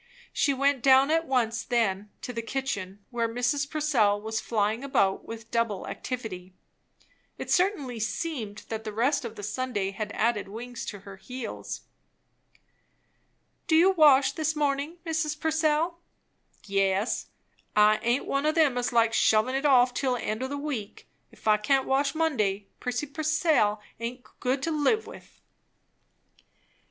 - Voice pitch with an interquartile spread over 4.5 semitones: Yes, average, 4.9 semitones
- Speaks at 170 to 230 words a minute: No, average, 155 wpm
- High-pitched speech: Yes, very high, 250 Hz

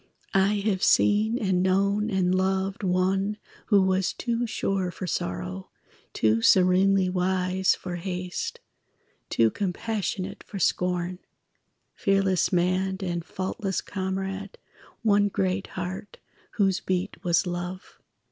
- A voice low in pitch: No, high, 190 Hz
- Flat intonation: Yes, narrow, 1.4 semitones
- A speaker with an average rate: No, slow, 115 wpm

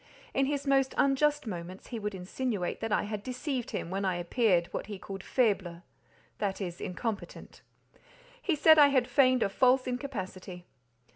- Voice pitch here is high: Yes, high, 220 Hz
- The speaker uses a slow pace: No, average, 160 wpm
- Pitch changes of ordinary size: No, wide, 5.9 semitones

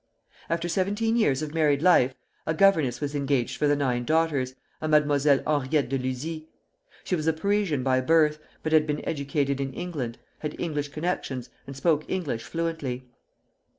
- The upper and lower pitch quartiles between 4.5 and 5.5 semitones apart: No, average, 3.2 semitones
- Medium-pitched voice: Yes, medium, 150 Hz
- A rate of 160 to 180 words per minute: Yes, average, 165 wpm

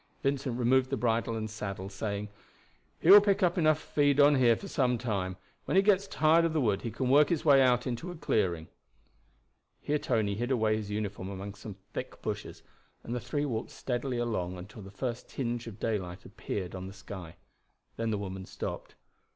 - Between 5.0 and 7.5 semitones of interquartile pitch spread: Yes, wide, 5.5 semitones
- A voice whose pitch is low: Yes, low, 115 Hz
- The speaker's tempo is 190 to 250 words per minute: Yes, average, 200 wpm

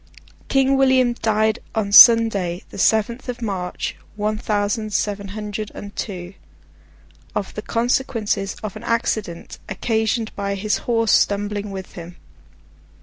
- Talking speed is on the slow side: Yes, slow, 130 wpm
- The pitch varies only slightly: Yes, narrow, 2.3 semitones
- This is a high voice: Yes, high, 215 Hz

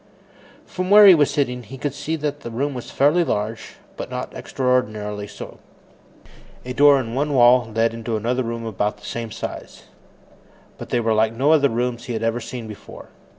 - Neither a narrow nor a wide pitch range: Yes, average, 3.7 semitones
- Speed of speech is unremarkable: Yes, average, 195 wpm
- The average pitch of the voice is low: Yes, low, 120 Hz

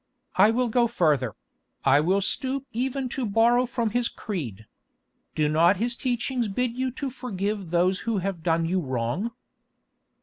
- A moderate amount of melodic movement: No, wide, 6.2 semitones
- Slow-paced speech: No, average, 160 wpm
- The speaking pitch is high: Yes, high, 210 Hz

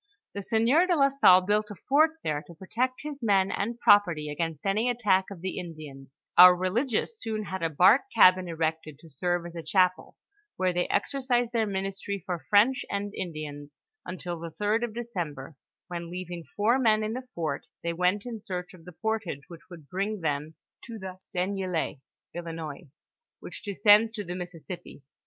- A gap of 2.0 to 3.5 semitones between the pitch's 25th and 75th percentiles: No, average, 4.5 semitones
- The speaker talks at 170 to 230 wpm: Yes, average, 180 wpm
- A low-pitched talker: No, medium, 185 Hz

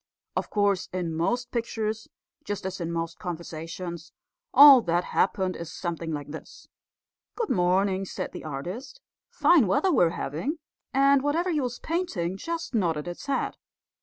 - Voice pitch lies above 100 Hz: Yes, high, 190 Hz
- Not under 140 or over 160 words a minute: Yes, average, 150 wpm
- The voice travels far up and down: Yes, wide, 7.6 semitones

